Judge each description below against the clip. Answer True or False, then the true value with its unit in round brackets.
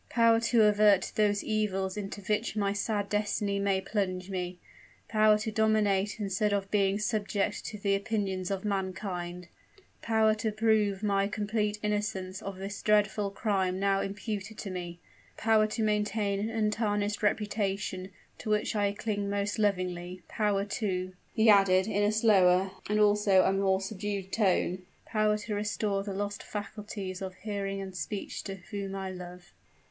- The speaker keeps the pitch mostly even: True (1.6 semitones)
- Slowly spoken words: False (160 wpm)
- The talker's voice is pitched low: False (205 Hz)